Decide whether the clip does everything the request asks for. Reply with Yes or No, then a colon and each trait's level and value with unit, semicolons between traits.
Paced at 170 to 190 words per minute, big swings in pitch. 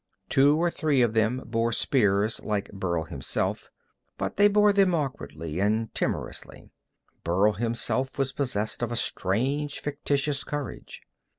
No: slow, 135 wpm; wide, 5.7 semitones